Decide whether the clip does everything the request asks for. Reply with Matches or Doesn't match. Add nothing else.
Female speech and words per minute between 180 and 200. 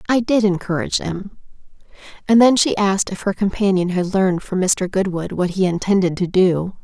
Matches